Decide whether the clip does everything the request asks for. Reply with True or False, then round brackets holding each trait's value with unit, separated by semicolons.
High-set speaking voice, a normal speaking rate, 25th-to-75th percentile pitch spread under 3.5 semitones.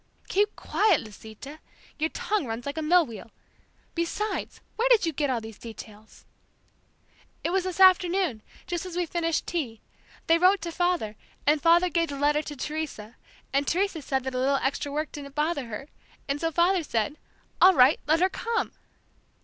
False (310 Hz; 180 wpm; 4.8 semitones)